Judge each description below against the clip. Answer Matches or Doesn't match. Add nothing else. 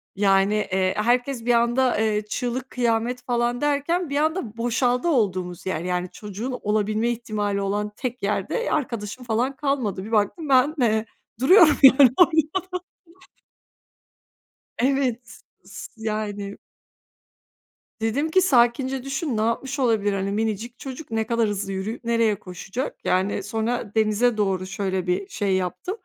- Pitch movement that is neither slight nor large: Matches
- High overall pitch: Matches